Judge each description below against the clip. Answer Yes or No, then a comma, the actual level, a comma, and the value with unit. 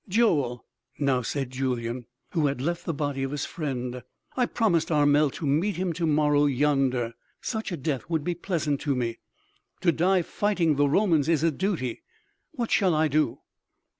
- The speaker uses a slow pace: No, average, 175 wpm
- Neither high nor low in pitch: Yes, medium, 150 Hz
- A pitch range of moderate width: Yes, average, 4.1 semitones